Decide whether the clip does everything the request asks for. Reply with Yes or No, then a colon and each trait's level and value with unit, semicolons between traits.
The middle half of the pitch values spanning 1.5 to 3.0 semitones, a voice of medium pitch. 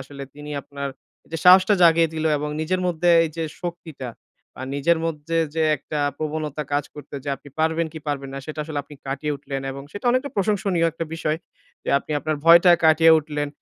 Yes: narrow, 2.4 semitones; medium, 155 Hz